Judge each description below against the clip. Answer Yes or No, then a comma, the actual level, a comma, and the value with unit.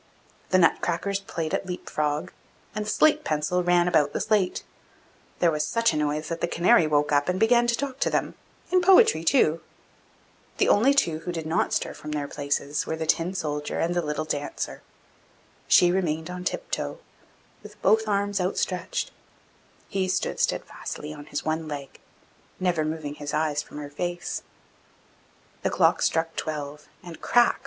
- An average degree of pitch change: Yes, average, 4.0 semitones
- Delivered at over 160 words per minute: Yes, average, 175 wpm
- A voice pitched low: No, medium, 165 Hz